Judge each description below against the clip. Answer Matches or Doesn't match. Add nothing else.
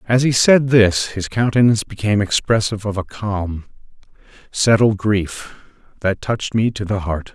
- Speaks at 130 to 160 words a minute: Matches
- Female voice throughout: Doesn't match